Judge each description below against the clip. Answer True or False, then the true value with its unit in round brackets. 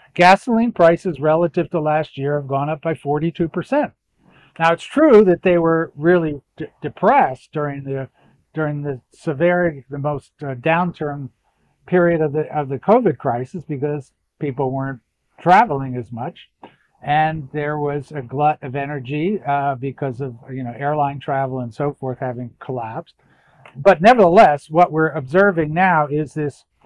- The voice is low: False (150 Hz)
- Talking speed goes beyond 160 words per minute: False (155 wpm)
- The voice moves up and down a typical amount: True (3.4 semitones)